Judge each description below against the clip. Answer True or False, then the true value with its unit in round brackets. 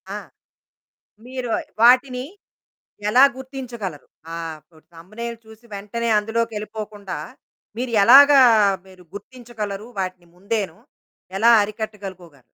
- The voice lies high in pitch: True (215 Hz)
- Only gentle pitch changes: False (3.7 semitones)